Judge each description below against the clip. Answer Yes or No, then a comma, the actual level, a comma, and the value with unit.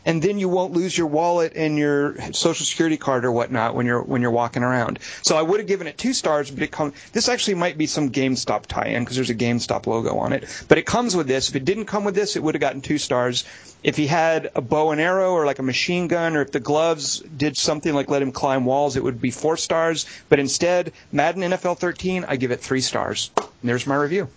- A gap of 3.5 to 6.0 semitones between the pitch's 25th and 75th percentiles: Yes, average, 4.7 semitones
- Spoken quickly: Yes, fast, 250 wpm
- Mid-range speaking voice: Yes, medium, 150 Hz